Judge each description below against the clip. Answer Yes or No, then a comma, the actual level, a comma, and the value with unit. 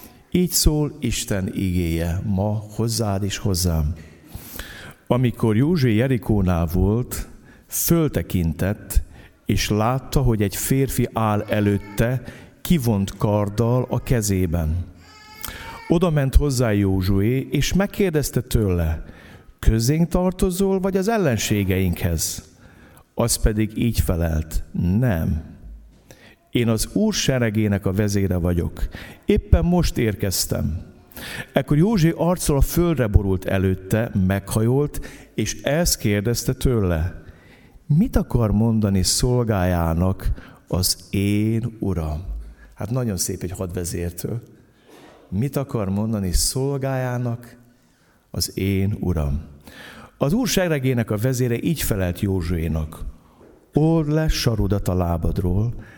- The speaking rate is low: Yes, slow, 100 wpm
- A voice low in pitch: Yes, low, 105 Hz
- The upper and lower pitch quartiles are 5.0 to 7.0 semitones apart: Yes, wide, 5.6 semitones